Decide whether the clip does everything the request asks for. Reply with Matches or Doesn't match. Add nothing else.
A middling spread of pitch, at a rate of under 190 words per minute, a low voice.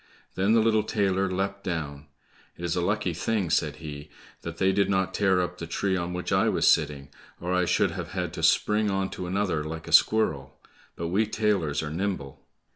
Doesn't match